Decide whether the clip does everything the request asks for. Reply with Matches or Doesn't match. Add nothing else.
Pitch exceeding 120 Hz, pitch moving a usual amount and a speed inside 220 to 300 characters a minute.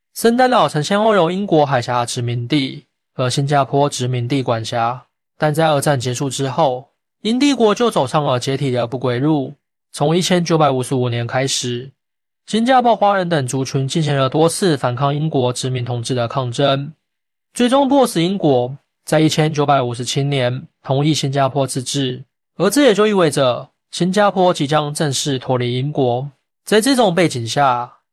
Matches